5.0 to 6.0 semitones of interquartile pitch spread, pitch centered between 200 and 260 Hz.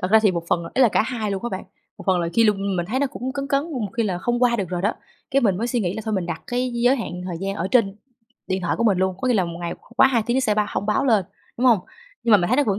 No: average, 4.6 semitones; high, 215 Hz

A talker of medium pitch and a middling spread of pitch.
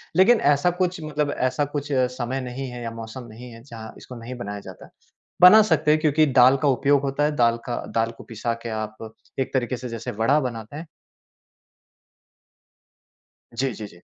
No: low, 130 Hz; average, 4.1 semitones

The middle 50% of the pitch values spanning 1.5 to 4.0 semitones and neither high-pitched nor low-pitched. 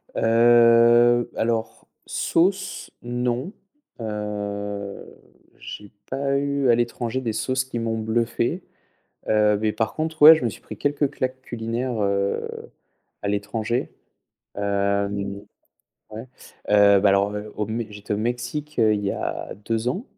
No: average, 3.1 semitones; low, 115 Hz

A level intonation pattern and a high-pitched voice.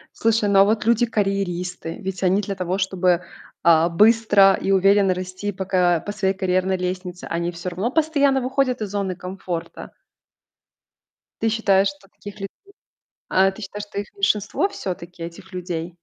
Yes: narrow, 2.3 semitones; high, 195 Hz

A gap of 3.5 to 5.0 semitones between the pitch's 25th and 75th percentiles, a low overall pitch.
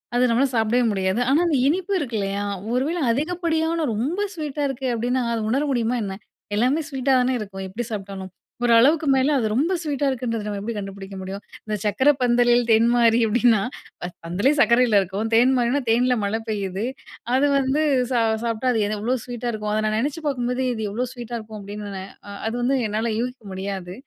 No: average, 3.9 semitones; high, 235 Hz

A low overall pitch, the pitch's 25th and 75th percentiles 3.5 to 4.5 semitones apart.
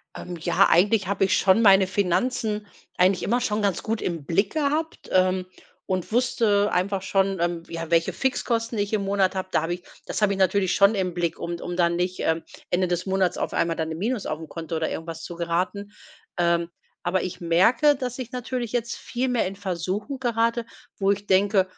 No: high, 190 Hz; average, 3.8 semitones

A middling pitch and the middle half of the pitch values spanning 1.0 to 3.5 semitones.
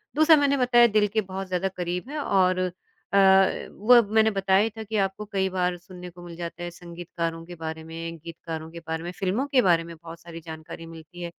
Yes: medium, 180 Hz; average, 2.9 semitones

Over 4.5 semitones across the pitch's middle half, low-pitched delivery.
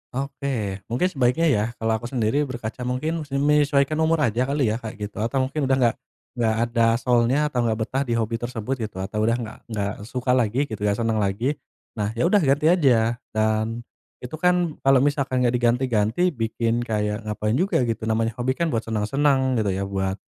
No: average, 3.8 semitones; low, 120 Hz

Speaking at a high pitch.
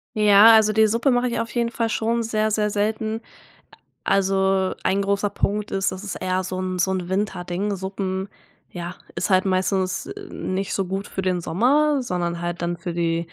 Yes: high, 195 Hz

